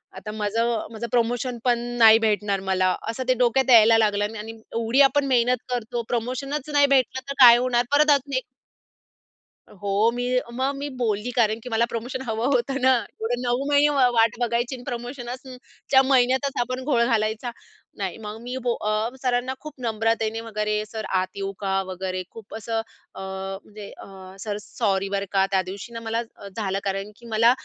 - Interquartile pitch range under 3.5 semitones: Yes, average, 3.0 semitones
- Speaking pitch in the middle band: No, high, 230 Hz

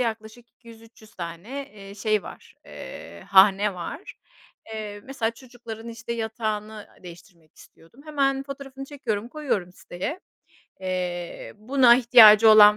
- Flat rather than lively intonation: No, average, 3.8 semitones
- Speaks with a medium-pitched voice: No, high, 220 Hz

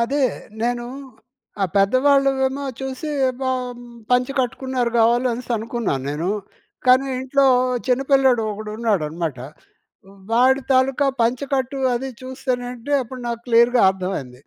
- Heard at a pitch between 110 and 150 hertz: No, very high, 250 Hz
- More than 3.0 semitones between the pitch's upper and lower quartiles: No, narrow, 2.6 semitones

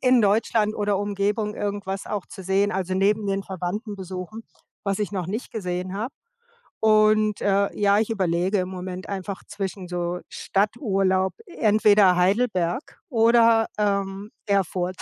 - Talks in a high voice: Yes, high, 200 Hz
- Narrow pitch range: Yes, narrow, 2.2 semitones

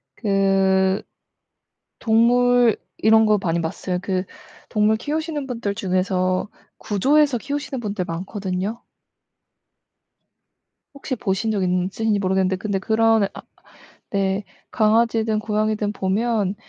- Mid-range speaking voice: No, high, 210 Hz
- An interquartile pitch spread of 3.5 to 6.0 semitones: No, average, 3.0 semitones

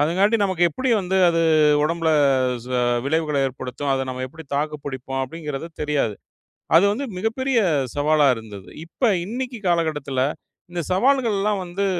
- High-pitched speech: No, medium, 165 Hz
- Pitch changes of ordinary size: No, wide, 5.8 semitones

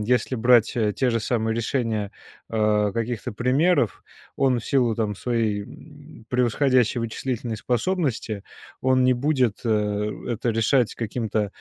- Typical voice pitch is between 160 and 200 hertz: No, low, 115 Hz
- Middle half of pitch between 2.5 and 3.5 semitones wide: Yes, average, 2.8 semitones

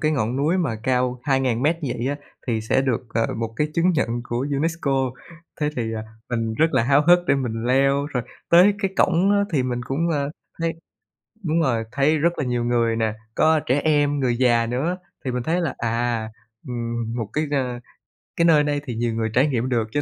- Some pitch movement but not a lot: Yes, average, 4.3 semitones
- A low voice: Yes, low, 130 Hz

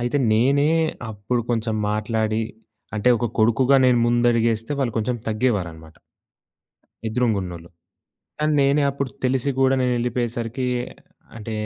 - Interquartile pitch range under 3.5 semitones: Yes, average, 2.7 semitones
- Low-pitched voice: Yes, low, 120 Hz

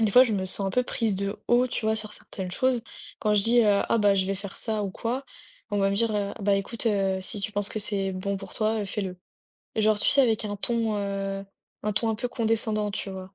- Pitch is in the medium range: No, high, 210 Hz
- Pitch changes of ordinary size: No, narrow, 2.2 semitones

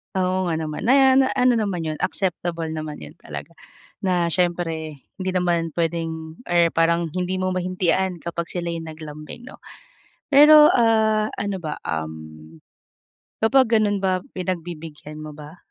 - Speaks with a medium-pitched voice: Yes, medium, 175 Hz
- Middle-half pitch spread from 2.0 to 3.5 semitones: Yes, average, 3.1 semitones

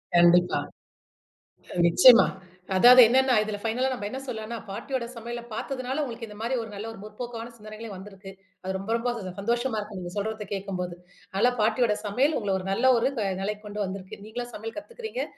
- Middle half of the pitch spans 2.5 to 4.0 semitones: Yes, average, 3.3 semitones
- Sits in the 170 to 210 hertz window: No, high, 220 Hz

